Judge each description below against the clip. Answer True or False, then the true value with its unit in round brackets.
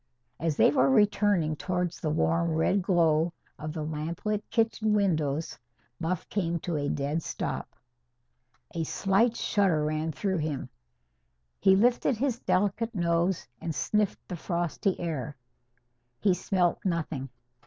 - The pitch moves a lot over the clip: False (4.2 semitones)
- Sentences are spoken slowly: True (130 wpm)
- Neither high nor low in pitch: True (170 Hz)